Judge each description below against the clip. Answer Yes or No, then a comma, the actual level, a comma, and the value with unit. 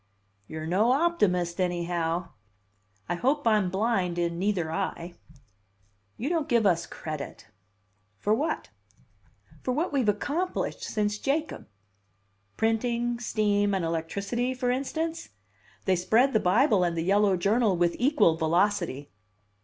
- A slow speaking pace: Yes, slow, 130 wpm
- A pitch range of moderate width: No, wide, 6.1 semitones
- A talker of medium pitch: No, high, 205 Hz